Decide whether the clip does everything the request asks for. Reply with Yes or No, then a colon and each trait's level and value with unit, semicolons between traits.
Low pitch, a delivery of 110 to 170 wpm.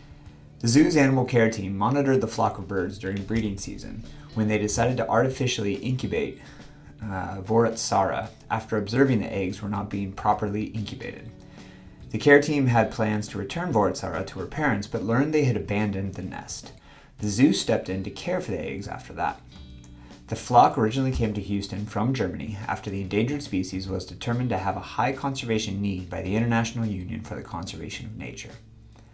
No: low, 105 Hz; average, 180 wpm